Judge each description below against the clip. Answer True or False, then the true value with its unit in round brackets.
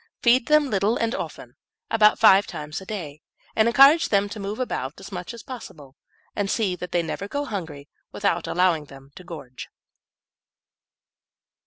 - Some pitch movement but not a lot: False (5.7 semitones)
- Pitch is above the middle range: True (195 Hz)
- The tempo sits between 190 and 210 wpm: False (165 wpm)